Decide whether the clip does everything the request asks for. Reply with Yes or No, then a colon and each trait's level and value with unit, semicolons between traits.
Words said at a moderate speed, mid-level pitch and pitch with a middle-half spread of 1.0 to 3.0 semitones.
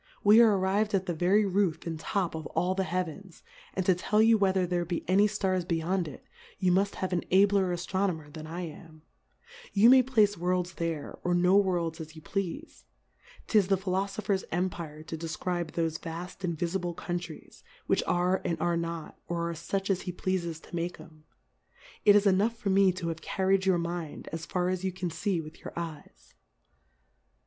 Yes: average, 190 wpm; medium, 180 Hz; narrow, 2.5 semitones